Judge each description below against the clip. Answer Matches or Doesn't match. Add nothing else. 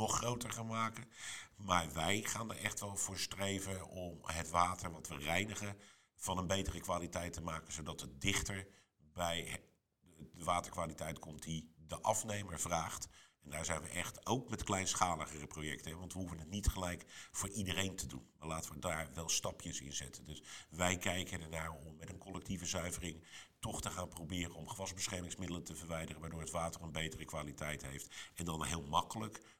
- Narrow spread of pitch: Doesn't match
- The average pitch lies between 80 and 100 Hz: Matches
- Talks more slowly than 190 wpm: Matches